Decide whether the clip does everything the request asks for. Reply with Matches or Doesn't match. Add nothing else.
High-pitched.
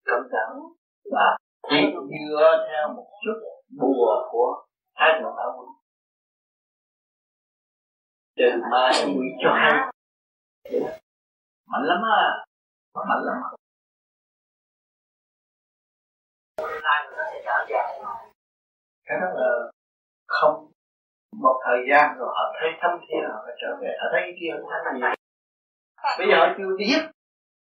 Doesn't match